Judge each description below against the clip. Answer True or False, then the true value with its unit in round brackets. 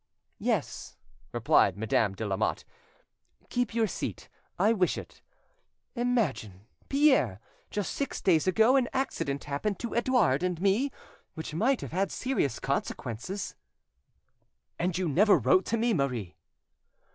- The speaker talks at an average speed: False (130 wpm)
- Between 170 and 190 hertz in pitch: True (185 Hz)